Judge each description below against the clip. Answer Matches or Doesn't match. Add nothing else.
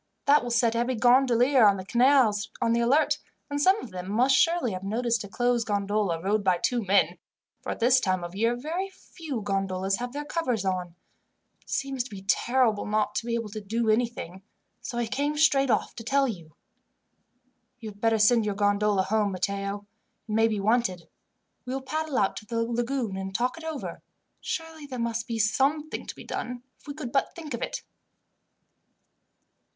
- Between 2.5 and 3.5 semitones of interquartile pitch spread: Doesn't match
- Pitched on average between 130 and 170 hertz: Doesn't match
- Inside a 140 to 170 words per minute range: Doesn't match